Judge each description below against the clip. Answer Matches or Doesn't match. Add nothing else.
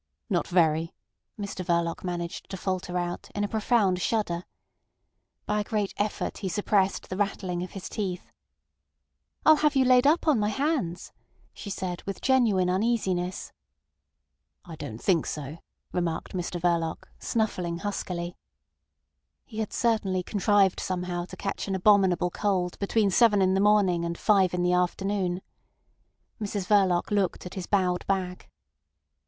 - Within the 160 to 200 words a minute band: Doesn't match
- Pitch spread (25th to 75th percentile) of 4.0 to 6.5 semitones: Doesn't match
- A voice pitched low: Doesn't match